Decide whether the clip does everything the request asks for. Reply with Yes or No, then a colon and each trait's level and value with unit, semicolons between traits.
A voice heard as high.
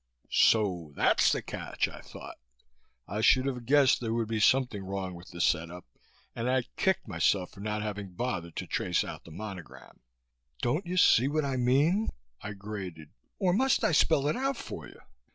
No: low, 110 Hz